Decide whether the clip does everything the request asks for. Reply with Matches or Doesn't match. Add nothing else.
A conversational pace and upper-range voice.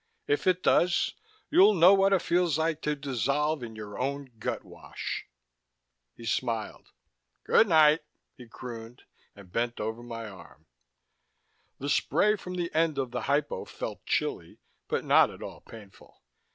Doesn't match